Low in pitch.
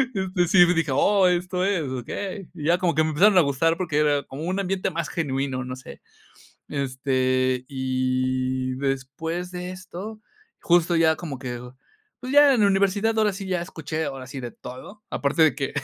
No: medium, 160 Hz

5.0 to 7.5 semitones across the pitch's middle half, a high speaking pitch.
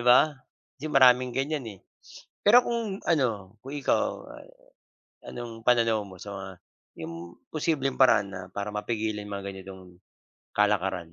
No: average, 5.3 semitones; low, 110 Hz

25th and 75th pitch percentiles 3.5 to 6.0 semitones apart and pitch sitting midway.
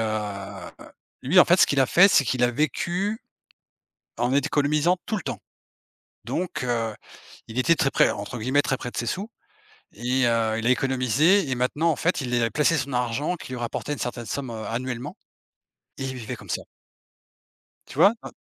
No: average, 4.2 semitones; low, 130 Hz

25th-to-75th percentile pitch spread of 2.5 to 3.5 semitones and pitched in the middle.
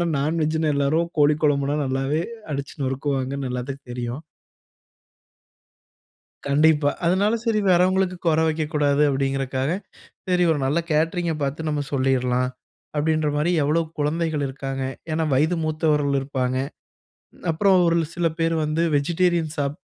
Yes: average, 3.0 semitones; medium, 150 Hz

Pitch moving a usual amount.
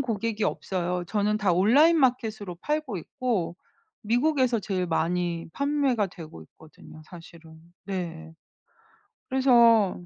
No: wide, 6.1 semitones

